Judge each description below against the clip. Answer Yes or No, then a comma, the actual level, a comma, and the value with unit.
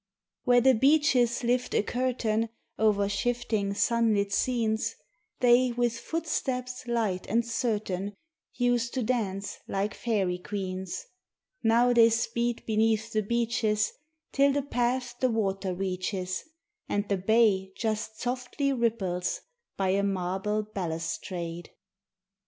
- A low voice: No, high, 220 Hz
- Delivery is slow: Yes, slow, 115 wpm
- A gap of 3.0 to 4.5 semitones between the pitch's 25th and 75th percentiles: Yes, average, 3.6 semitones